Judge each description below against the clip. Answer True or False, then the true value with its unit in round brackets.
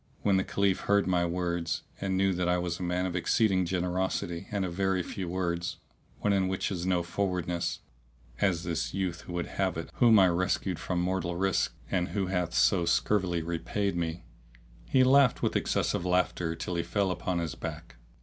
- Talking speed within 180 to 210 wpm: True (190 wpm)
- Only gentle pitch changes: True (1.8 semitones)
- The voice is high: False (90 Hz)